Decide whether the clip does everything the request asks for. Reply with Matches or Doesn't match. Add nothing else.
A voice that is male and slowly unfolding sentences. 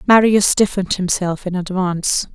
Doesn't match